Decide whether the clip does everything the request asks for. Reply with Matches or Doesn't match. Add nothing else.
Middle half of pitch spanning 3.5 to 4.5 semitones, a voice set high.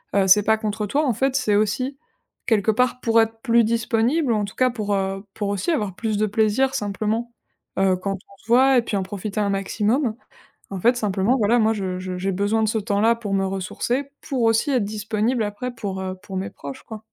Doesn't match